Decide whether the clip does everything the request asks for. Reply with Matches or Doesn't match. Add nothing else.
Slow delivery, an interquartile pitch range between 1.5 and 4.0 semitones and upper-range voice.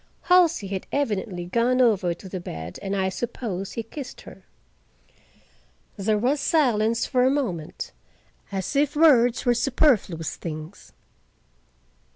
Doesn't match